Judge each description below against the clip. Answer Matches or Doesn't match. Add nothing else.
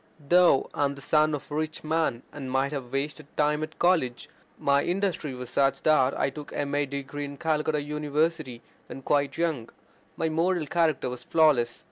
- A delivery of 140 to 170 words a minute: Doesn't match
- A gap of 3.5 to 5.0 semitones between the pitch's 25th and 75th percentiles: Doesn't match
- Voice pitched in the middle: Matches